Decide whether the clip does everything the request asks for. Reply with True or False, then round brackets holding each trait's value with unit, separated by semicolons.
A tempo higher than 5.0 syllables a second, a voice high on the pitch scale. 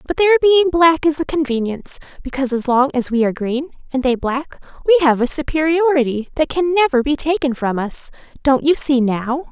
True (5.5 syllables/s; 285 Hz)